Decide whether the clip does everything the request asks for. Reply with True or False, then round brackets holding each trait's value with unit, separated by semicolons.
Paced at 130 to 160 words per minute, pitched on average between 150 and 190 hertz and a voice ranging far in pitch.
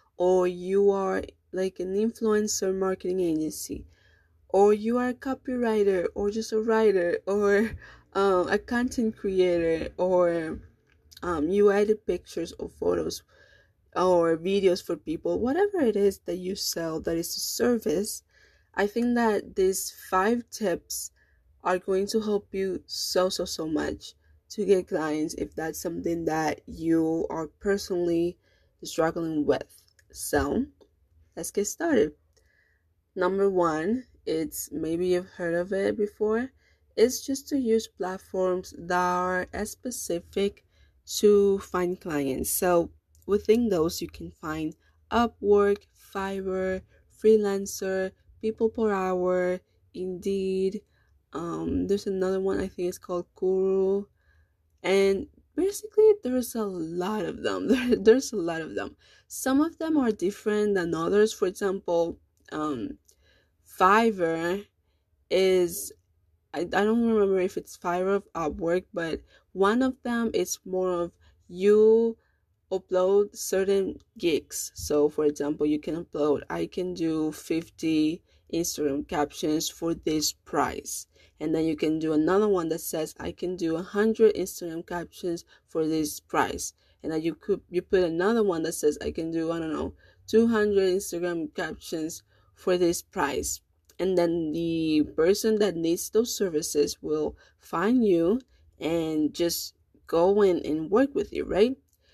False (140 wpm; 185 Hz; 4.2 semitones)